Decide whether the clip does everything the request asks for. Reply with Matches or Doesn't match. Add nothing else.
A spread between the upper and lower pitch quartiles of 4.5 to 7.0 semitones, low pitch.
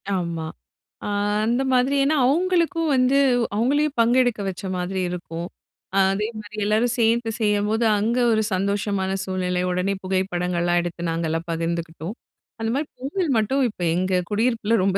Doesn't match